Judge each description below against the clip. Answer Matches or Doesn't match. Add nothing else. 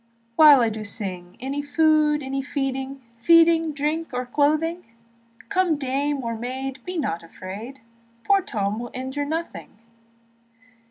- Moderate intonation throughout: Matches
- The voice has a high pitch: Matches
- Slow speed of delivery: Matches